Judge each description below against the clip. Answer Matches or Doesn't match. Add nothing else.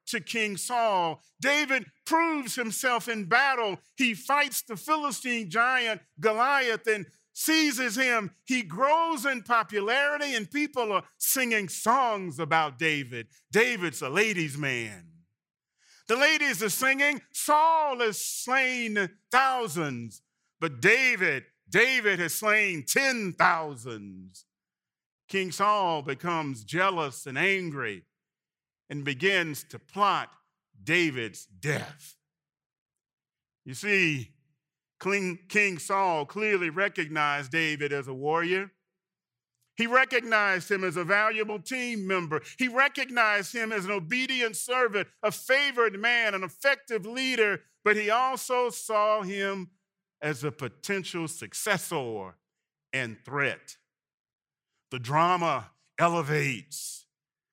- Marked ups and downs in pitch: Matches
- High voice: Matches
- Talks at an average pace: Doesn't match